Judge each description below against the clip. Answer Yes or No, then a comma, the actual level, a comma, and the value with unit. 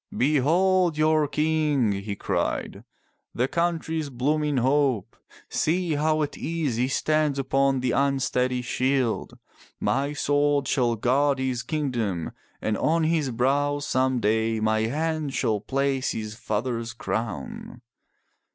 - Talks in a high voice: No, low, 135 Hz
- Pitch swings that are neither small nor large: Yes, average, 4.1 semitones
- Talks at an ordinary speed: No, slow, 125 wpm